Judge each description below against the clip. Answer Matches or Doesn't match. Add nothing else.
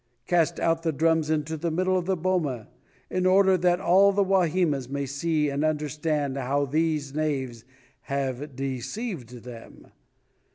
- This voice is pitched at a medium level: Matches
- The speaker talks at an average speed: Matches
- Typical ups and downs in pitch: Matches